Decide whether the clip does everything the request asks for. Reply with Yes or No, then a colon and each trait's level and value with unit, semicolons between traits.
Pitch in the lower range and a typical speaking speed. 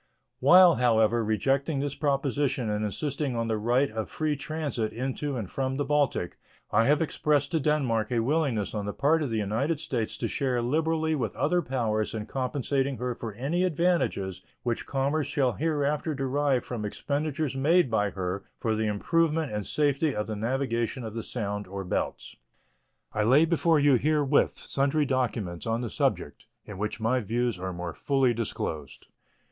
Yes: low, 130 Hz; average, 175 wpm